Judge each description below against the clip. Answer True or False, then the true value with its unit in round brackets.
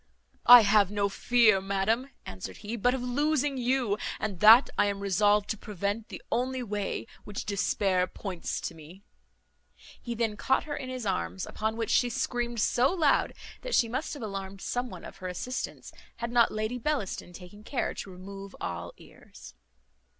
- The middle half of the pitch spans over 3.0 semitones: True (3.9 semitones)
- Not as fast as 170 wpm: False (175 wpm)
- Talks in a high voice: True (215 Hz)